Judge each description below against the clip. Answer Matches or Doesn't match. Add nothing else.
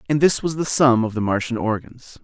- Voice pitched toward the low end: Matches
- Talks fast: Matches